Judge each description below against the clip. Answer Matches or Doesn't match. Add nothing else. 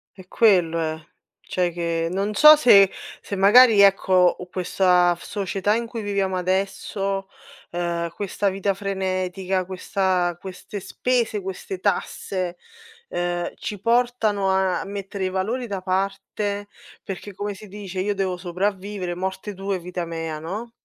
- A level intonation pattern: Matches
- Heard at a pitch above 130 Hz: Matches